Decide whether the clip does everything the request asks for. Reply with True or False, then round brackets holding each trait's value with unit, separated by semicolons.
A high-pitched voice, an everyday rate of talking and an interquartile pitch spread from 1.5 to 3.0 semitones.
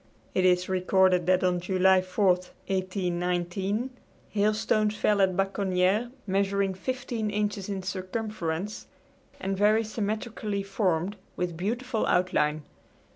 False (195 Hz; 110 wpm; 2.5 semitones)